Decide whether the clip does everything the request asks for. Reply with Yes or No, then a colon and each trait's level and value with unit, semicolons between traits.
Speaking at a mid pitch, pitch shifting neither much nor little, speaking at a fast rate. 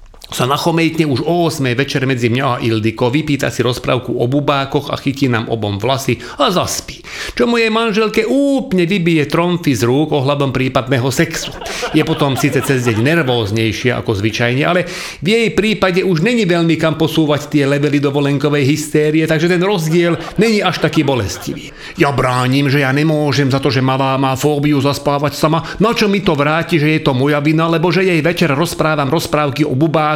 Yes: medium, 150 Hz; average, 3.8 semitones; fast, 185 wpm